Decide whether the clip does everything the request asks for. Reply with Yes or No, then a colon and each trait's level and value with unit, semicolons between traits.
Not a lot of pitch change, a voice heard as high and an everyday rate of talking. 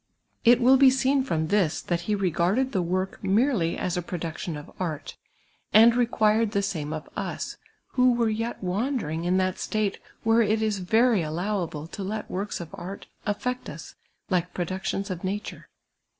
No: average, 4.4 semitones; high, 195 Hz; average, 175 wpm